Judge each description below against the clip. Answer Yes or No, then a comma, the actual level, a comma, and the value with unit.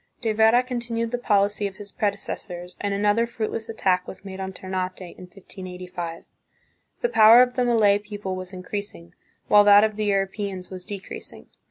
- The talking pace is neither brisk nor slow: Yes, average, 170 wpm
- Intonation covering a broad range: No, average, 2.8 semitones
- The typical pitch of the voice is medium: No, high, 205 Hz